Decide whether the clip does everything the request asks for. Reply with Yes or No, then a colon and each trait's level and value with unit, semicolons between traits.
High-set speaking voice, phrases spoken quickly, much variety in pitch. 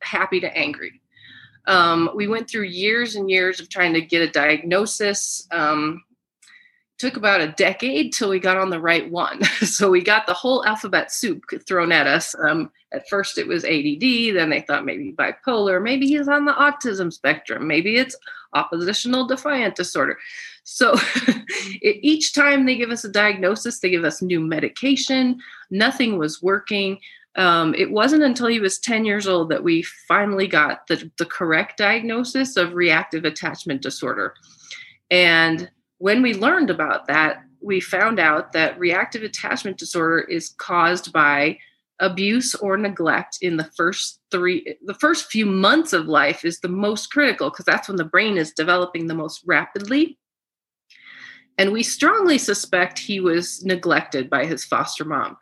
No: high, 200 Hz; average, 165 wpm; wide, 6.6 semitones